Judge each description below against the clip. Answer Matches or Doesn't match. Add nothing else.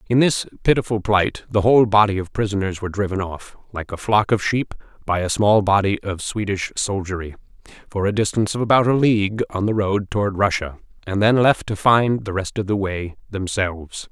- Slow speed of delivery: Doesn't match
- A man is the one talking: Matches